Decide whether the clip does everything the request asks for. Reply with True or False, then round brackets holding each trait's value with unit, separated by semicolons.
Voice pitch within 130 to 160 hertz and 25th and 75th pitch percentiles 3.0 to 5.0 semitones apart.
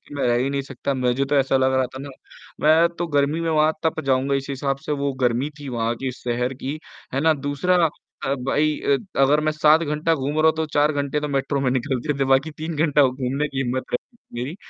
False (140 Hz; 2.4 semitones)